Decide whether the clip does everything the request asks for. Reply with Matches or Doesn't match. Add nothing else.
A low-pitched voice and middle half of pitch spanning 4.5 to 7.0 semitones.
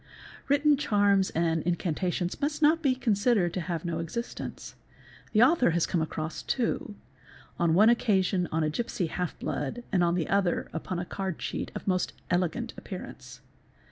Doesn't match